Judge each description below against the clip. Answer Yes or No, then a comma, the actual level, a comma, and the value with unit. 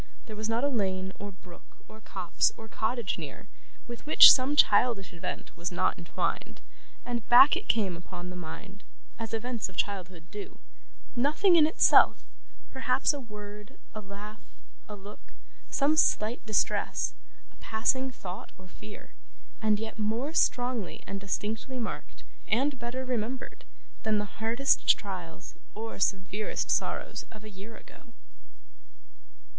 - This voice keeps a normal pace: Yes, average, 145 wpm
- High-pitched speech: Yes, high, 215 Hz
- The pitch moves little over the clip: No, average, 3.9 semitones